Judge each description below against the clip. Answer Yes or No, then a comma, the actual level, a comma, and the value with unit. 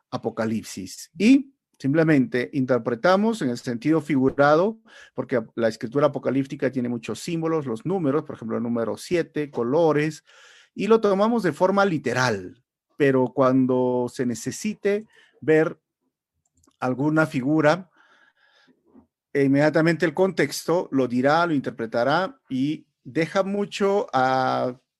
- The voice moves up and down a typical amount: No, wide, 5.7 semitones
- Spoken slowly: Yes, slow, 115 wpm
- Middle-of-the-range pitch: Yes, medium, 150 Hz